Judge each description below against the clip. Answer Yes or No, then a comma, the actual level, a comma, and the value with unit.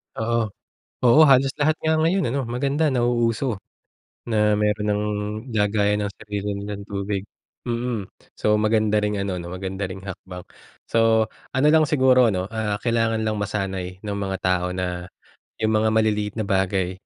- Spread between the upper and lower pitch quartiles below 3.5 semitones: Yes, average, 3.0 semitones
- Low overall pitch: Yes, low, 105 Hz